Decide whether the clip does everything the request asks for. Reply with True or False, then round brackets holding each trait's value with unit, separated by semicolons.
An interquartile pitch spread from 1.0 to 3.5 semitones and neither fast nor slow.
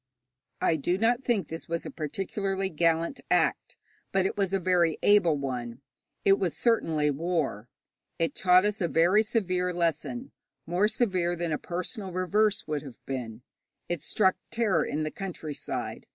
False (3.9 semitones; 160 wpm)